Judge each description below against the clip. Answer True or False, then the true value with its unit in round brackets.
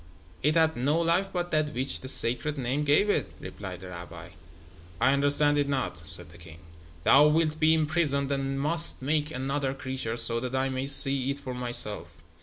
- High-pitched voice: False (140 Hz)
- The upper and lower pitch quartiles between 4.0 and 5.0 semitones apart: False (3.1 semitones)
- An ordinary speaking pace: True (190 wpm)